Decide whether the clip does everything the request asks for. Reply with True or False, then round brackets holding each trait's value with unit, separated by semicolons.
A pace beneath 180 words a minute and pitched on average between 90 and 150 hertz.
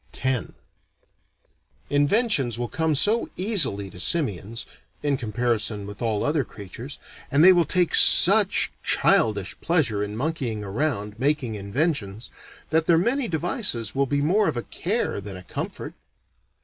True (140 wpm; 135 Hz)